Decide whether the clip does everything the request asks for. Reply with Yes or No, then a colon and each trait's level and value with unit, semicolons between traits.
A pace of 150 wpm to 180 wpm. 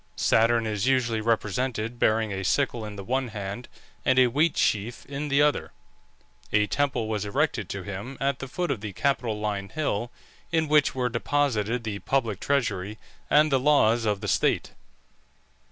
Yes: average, 170 wpm